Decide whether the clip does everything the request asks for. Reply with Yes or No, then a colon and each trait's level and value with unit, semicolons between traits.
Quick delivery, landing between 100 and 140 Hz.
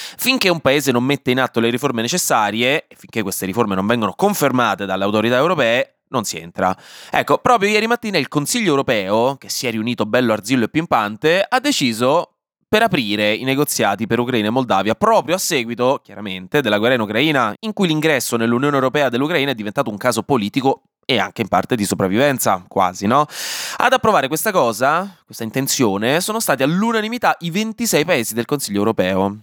Yes: fast, 185 wpm; low, 135 Hz